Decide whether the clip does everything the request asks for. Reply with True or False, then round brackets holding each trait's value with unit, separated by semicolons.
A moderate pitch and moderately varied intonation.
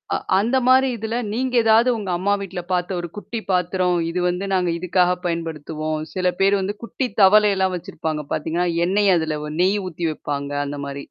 True (180 Hz; 3.5 semitones)